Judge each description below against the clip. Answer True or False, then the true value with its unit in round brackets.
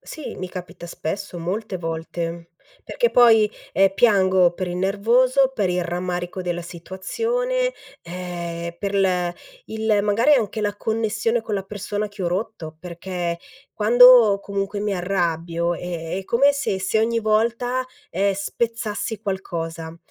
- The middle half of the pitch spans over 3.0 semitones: True (4.0 semitones)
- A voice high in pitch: True (195 Hz)